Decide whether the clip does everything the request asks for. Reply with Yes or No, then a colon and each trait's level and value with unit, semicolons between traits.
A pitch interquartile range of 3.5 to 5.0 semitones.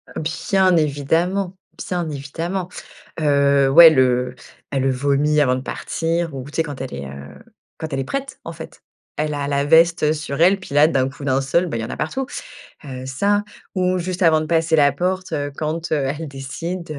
Yes: average, 3.9 semitones